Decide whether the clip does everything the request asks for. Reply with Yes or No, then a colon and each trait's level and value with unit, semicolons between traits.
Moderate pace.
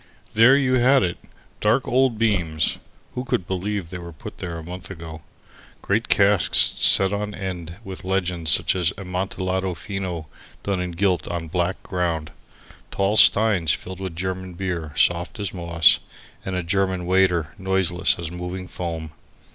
Yes: average, 160 wpm